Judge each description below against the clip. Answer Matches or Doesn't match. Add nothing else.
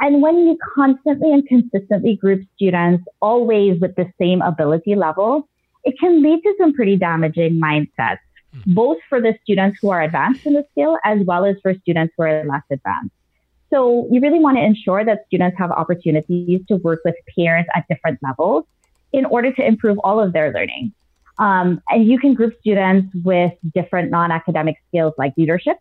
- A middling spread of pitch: Doesn't match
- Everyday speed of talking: Matches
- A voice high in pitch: Matches